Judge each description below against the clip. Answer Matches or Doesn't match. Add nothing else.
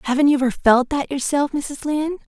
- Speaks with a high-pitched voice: Matches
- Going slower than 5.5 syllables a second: Doesn't match